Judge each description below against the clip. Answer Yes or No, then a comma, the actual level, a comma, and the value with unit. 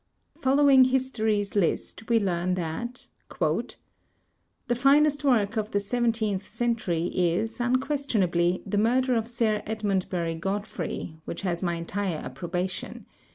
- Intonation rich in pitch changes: No, average, 5.0 semitones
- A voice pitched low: No, high, 210 Hz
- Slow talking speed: Yes, slow, 120 wpm